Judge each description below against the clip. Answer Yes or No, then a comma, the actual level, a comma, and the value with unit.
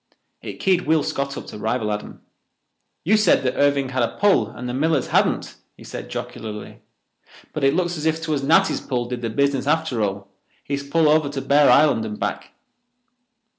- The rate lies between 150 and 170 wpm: No, average, 185 wpm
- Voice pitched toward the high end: No, medium, 140 Hz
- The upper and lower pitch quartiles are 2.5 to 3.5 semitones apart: No, average, 4.5 semitones